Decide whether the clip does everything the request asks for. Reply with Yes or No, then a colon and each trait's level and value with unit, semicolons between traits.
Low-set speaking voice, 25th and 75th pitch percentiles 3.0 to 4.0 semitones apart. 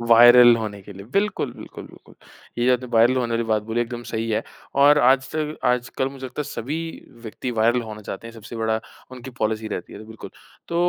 No: low, 120 Hz; narrow, 2.5 semitones